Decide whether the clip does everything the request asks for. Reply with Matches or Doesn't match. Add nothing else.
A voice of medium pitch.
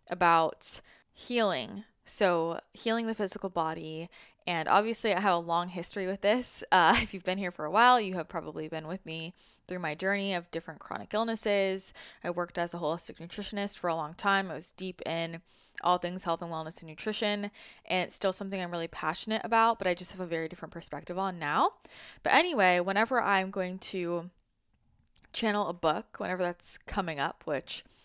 Matches